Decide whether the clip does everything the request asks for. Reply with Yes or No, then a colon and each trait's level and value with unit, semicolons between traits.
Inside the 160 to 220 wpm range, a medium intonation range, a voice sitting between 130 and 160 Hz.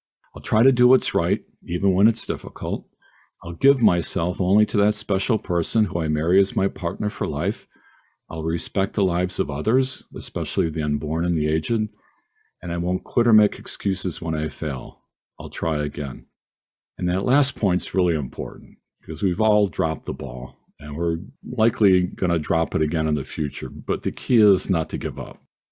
No: average, 190 wpm; average, 4.3 semitones; very low, 90 Hz